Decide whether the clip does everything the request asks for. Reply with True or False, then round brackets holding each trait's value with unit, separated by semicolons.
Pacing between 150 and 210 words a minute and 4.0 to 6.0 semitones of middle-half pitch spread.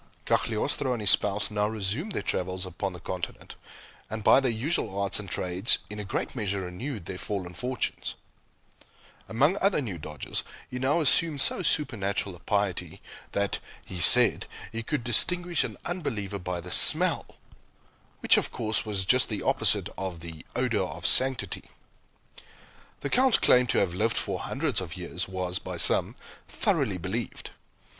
True (160 wpm; 5.5 semitones)